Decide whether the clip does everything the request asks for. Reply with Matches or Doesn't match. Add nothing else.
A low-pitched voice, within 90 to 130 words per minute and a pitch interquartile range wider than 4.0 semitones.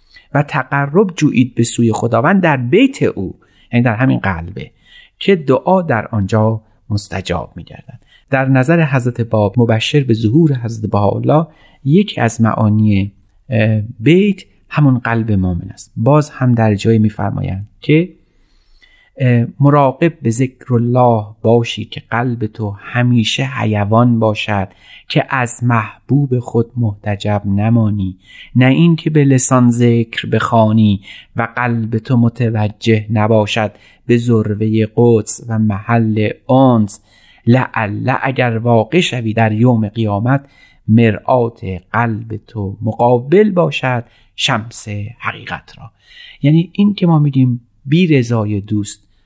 Doesn't match